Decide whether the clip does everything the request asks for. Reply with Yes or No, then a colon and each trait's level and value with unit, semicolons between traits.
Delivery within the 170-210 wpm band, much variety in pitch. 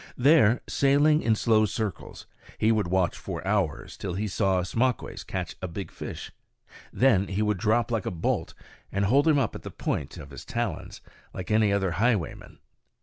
No: average, 180 wpm; average, 4.0 semitones